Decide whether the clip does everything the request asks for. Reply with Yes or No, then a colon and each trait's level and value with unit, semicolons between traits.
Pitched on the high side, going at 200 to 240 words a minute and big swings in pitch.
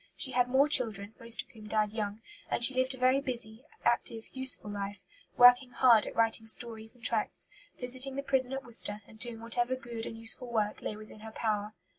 No: high, 230 Hz; fast, 205 wpm; average, 2.7 semitones